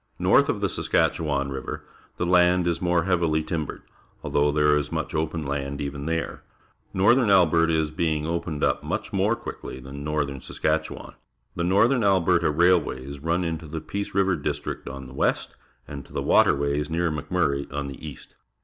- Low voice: Yes, very low, 80 Hz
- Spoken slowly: No, average, 165 wpm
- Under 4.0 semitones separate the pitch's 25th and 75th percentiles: Yes, average, 3.3 semitones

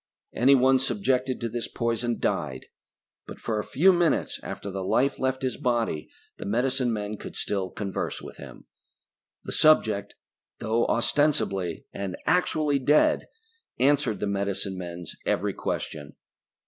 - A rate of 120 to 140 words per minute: Yes, slow, 135 wpm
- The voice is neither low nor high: No, low, 115 Hz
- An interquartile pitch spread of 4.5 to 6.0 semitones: Yes, average, 5.0 semitones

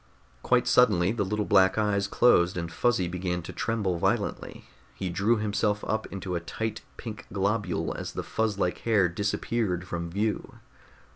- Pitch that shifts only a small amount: No, average, 3.3 semitones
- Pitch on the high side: No, low, 100 Hz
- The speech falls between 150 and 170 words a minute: Yes, average, 160 wpm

